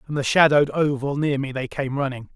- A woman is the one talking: No, male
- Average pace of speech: No, fast, 230 wpm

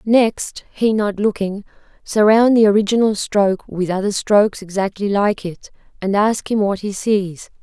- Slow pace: No, average, 155 wpm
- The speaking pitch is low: No, high, 205 Hz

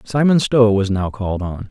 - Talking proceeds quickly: Yes, fast, 210 wpm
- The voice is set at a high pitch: No, low, 110 Hz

